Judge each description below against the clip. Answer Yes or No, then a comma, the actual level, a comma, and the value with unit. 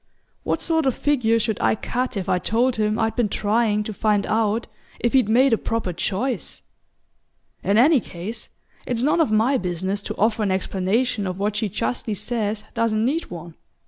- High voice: Yes, high, 220 Hz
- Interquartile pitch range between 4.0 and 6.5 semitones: No, average, 2.9 semitones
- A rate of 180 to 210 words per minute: Yes, average, 185 wpm